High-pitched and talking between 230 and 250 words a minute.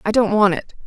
No: high, 205 Hz; fast, 275 wpm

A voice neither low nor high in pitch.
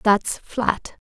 No: high, 215 Hz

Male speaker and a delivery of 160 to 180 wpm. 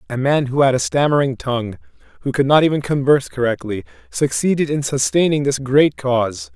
Yes: male; average, 175 wpm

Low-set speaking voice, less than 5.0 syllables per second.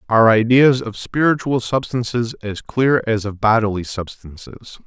Yes: low, 115 Hz; 4.4 syllables/s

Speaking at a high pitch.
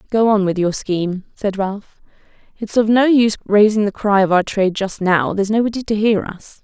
Yes: high, 205 Hz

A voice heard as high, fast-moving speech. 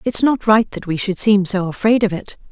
Yes: high, 205 Hz; fast, 260 wpm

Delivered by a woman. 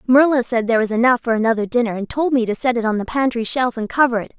Yes: female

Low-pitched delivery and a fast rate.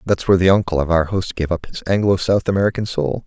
Yes: very low, 90 Hz; fast, 255 wpm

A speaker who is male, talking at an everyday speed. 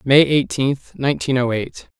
Yes: male; average, 150 wpm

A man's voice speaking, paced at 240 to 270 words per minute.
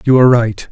Yes: male; fast, 255 wpm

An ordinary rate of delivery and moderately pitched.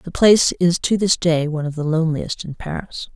No: fast, 230 wpm; medium, 165 Hz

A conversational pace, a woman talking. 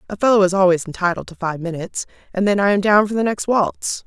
No: fast, 250 wpm; female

